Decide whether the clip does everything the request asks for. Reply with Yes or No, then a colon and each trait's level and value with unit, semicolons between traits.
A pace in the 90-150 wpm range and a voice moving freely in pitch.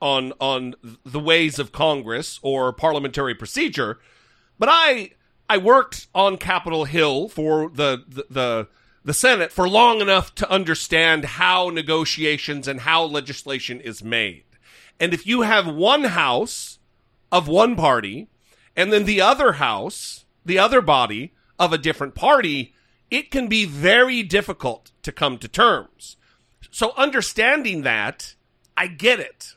Yes: average, 140 wpm; wide, 6.4 semitones